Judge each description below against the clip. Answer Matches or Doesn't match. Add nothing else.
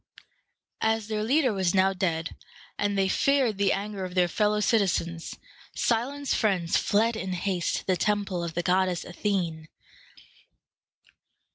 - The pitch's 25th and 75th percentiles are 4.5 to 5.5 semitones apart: Doesn't match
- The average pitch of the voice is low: Doesn't match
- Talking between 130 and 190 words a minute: Matches